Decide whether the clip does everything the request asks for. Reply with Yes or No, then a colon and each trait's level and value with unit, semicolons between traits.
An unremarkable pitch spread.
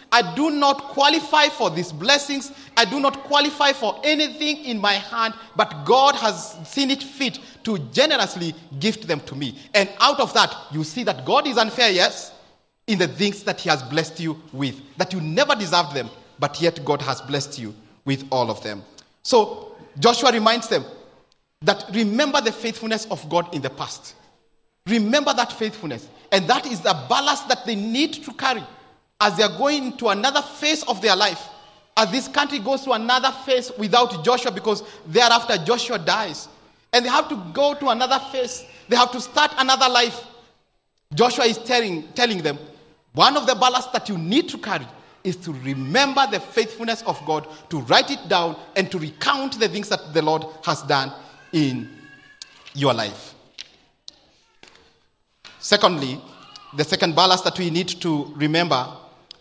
No: wide, 7.9 semitones